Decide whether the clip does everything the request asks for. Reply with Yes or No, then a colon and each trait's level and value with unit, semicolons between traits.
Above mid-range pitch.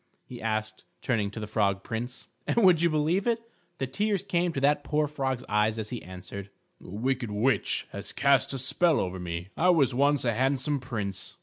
No: low, 125 Hz